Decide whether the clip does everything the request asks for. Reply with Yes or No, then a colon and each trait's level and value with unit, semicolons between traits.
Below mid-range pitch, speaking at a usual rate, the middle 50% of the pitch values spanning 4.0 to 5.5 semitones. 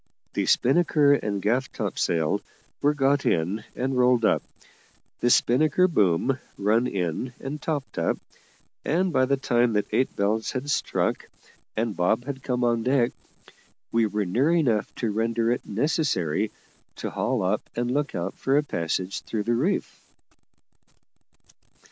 Yes: low, 120 Hz; average, 150 wpm; average, 4.8 semitones